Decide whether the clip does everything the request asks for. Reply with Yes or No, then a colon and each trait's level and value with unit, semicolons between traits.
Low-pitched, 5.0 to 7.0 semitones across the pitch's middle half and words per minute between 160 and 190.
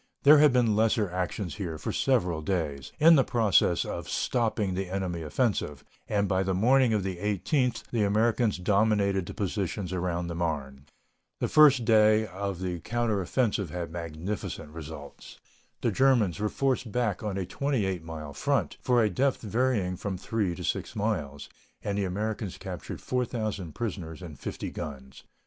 No: low, 100 Hz; average, 4.5 semitones; average, 165 wpm